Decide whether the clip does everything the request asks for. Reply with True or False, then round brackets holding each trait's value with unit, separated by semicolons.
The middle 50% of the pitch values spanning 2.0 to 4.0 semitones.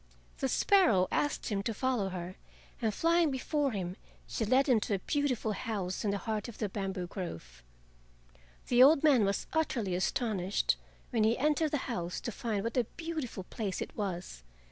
False (5.6 semitones)